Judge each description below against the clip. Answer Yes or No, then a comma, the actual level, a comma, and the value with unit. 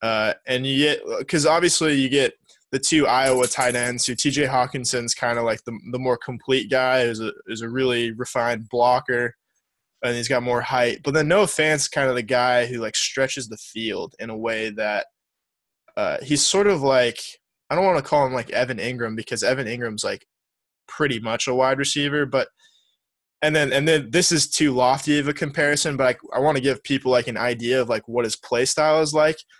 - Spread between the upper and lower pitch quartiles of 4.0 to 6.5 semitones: No, average, 3.5 semitones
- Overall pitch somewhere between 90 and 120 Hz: No, low, 130 Hz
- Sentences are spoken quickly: Yes, fast, 215 wpm